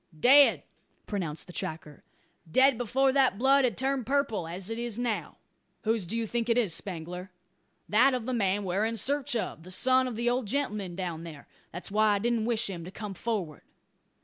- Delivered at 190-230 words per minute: Yes, average, 200 wpm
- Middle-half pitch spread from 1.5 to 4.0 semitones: No, average, 5.3 semitones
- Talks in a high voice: Yes, high, 220 Hz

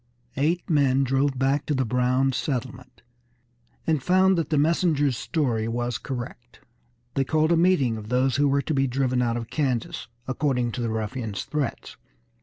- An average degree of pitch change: Yes, average, 3.3 semitones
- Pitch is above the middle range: No, low, 135 Hz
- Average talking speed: Yes, average, 170 wpm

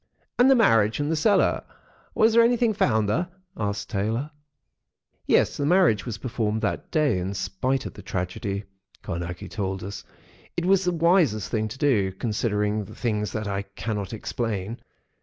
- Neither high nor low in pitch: No, low, 110 Hz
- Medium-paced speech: Yes, average, 160 wpm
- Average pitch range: No, wide, 7.1 semitones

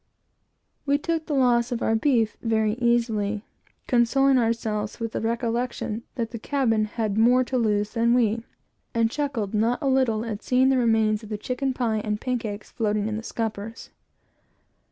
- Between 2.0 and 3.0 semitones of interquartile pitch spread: Yes, narrow, 2.5 semitones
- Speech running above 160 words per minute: Yes, average, 175 wpm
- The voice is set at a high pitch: Yes, high, 230 Hz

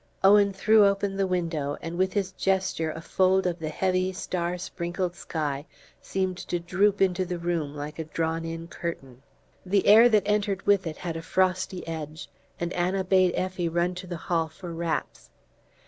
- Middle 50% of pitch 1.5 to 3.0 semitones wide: Yes, narrow, 2.5 semitones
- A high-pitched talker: No, medium, 180 Hz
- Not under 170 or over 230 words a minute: Yes, average, 180 wpm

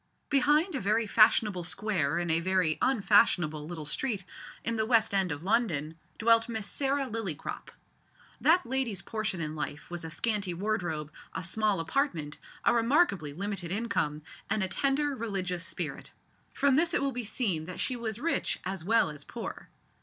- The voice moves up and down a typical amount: No, wide, 5.7 semitones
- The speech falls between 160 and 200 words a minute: Yes, average, 170 wpm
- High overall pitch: Yes, high, 205 Hz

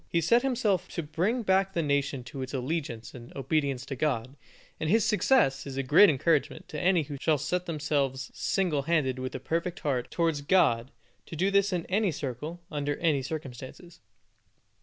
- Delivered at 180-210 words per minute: Yes, average, 185 wpm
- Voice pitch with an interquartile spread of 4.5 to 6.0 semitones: Yes, average, 4.8 semitones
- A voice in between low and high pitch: Yes, medium, 155 Hz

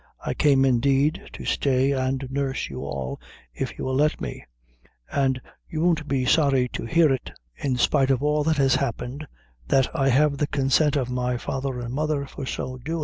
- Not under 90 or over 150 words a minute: No, average, 195 wpm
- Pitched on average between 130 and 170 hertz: Yes, low, 135 Hz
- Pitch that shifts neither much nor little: No, narrow, 2.2 semitones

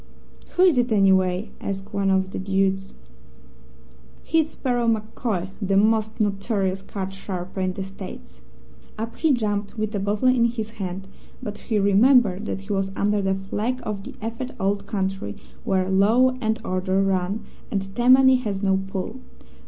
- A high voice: Yes, high, 200 Hz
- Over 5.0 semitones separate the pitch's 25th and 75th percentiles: No, average, 2.7 semitones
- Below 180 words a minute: Yes, average, 160 wpm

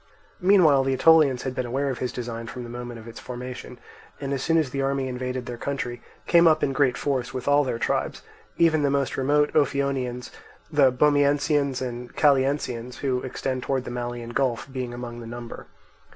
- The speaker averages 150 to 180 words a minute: No, average, 195 wpm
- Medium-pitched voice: No, low, 130 Hz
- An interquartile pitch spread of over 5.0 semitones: No, narrow, 2.5 semitones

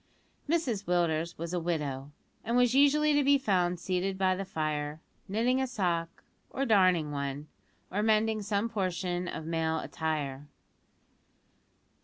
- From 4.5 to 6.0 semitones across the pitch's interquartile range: Yes, wide, 5.6 semitones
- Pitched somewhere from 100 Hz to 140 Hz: No, medium, 180 Hz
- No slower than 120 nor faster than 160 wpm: Yes, average, 140 wpm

